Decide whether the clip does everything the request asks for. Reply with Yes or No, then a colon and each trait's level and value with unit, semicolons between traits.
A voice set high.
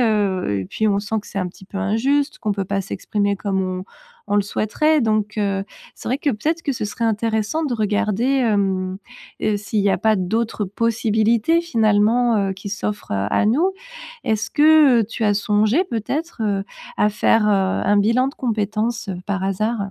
Yes: high, 215 Hz